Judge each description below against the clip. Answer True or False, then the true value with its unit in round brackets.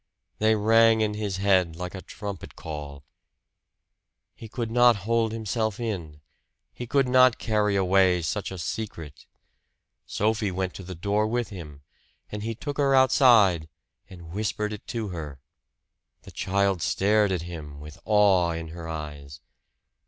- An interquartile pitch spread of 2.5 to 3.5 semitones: False (4.7 semitones)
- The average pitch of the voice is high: False (100 Hz)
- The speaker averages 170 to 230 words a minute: False (150 wpm)